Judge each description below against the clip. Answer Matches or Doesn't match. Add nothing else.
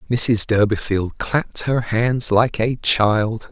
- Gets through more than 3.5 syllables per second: Doesn't match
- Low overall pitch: Matches